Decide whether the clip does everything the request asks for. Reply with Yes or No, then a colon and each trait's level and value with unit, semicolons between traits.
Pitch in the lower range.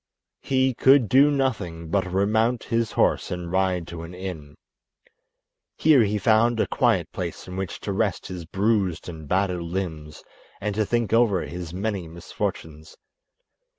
Yes: very low, 95 Hz